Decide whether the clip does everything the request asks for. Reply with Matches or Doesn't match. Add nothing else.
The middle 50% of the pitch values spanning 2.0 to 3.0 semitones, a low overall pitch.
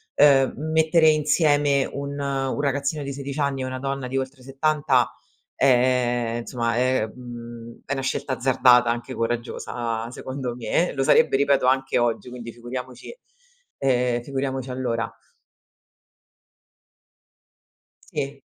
Matches